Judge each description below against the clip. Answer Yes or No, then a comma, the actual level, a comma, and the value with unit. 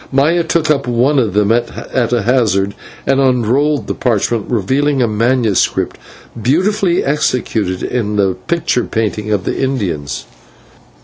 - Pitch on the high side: No, low, 120 Hz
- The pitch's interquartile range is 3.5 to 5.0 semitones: Yes, average, 4.6 semitones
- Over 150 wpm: No, slow, 135 wpm